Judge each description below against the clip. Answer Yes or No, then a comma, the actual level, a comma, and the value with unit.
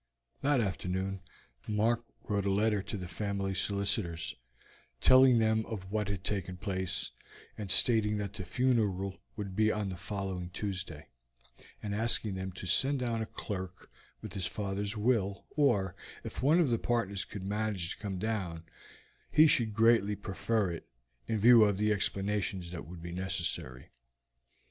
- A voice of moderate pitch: No, low, 100 Hz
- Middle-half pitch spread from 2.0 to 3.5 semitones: Yes, average, 2.7 semitones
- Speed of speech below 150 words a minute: No, average, 160 wpm